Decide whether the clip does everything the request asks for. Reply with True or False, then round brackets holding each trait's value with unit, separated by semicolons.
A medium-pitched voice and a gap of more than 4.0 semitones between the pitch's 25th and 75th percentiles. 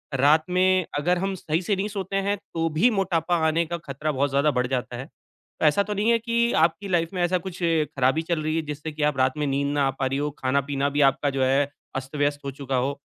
True (155 Hz; 4.5 semitones)